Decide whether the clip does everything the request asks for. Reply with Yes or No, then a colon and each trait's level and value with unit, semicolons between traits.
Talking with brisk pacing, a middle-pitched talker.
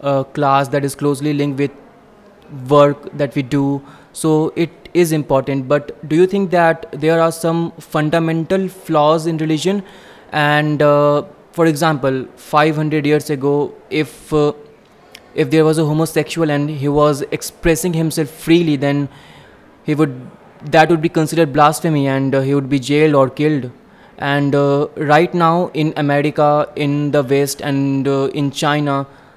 No: average, 155 wpm; medium, 150 Hz